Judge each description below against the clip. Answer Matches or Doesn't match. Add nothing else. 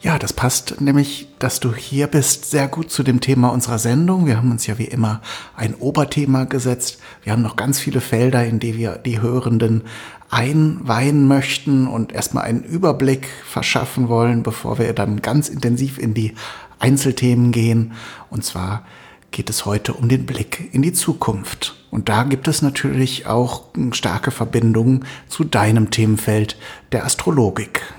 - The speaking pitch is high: Doesn't match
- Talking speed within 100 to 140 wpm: Doesn't match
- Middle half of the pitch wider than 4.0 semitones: Doesn't match